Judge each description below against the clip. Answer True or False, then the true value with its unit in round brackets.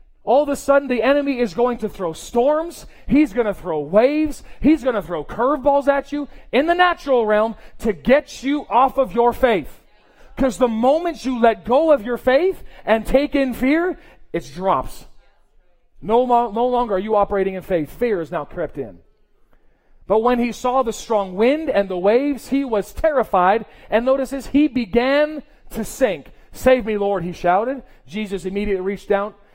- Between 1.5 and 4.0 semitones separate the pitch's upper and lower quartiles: False (5.1 semitones)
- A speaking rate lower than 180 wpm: False (185 wpm)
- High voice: True (245 Hz)